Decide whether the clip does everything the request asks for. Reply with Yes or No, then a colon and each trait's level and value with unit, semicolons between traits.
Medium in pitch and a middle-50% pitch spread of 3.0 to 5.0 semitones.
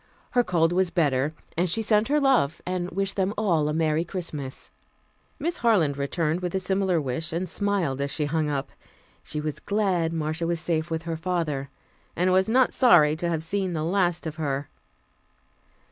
Yes: medium, 170 Hz; average, 3.6 semitones